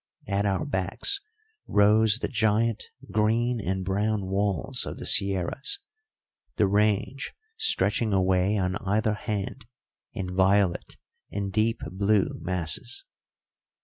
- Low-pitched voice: Yes, low, 100 Hz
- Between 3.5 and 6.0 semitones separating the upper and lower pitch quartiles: No, narrow, 2.4 semitones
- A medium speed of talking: No, slow, 115 wpm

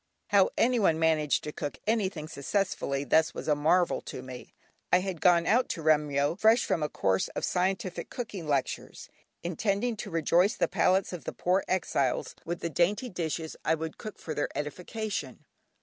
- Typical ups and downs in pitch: Yes, average, 4.3 semitones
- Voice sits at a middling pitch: Yes, medium, 170 Hz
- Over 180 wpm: No, average, 175 wpm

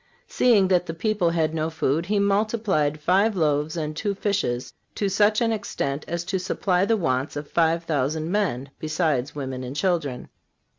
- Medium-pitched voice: Yes, medium, 165 Hz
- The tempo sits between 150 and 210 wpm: Yes, average, 170 wpm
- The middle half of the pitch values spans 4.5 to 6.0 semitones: Yes, average, 5.2 semitones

